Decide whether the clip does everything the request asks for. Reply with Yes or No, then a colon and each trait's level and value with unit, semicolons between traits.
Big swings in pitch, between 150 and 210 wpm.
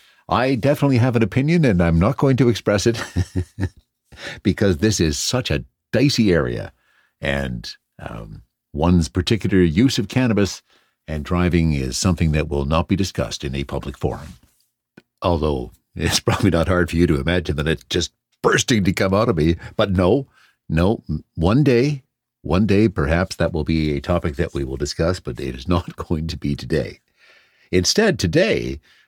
Yes: wide, 5.7 semitones; average, 175 wpm